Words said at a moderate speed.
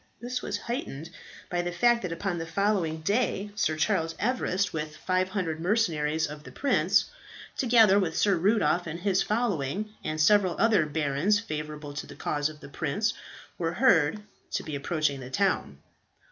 Yes: average, 165 wpm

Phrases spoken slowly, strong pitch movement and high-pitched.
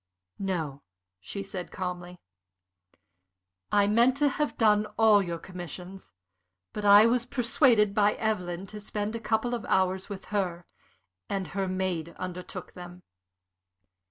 No: slow, 130 wpm; average, 3.2 semitones; high, 195 Hz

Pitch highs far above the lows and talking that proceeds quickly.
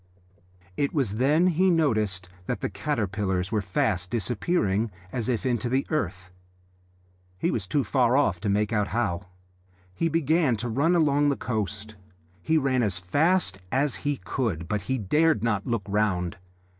No: wide, 6.3 semitones; average, 160 wpm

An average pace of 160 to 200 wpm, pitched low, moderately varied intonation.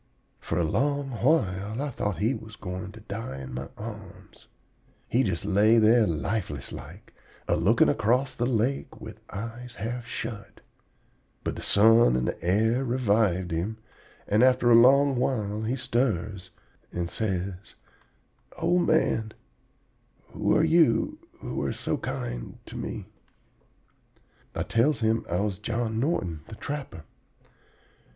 No: average, 140 wpm; low, 110 Hz; average, 4.2 semitones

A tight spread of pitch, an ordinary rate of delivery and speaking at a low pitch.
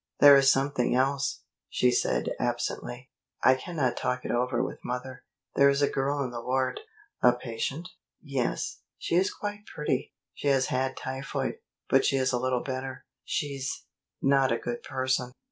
Yes: narrow, 1.8 semitones; average, 170 wpm; low, 130 Hz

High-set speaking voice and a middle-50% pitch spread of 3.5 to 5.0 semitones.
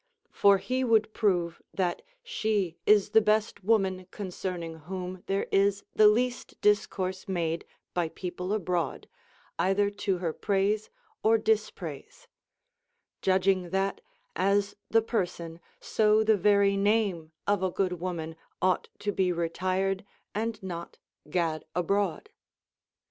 No: high, 195 Hz; average, 2.7 semitones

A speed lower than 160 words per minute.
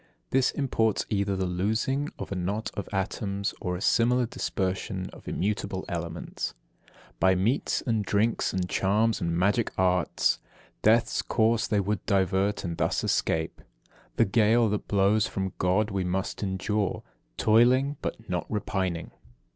Yes: average, 145 wpm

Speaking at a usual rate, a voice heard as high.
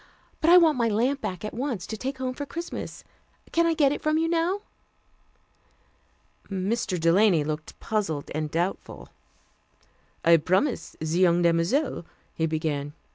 Yes: average, 155 wpm; high, 210 Hz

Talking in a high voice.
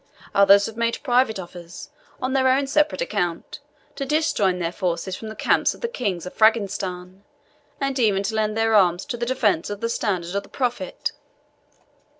Yes: high, 210 Hz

